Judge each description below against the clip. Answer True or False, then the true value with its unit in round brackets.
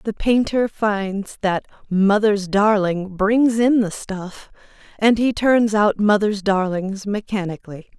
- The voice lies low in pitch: False (205 Hz)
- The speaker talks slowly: True (130 wpm)